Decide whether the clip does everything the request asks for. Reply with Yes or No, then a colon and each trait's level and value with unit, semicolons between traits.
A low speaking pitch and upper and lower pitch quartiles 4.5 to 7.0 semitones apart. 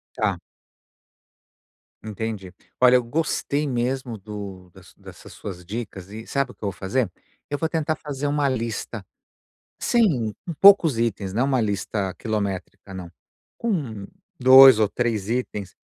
Yes: low, 115 Hz; average, 5.0 semitones